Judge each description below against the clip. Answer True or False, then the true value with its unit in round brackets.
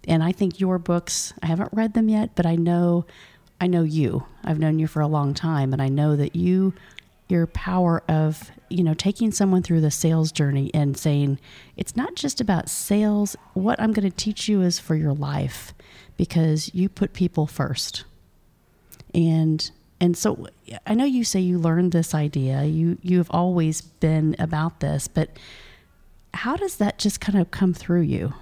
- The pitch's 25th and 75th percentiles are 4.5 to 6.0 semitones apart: False (3.7 semitones)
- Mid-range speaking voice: True (170 Hz)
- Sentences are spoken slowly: False (185 wpm)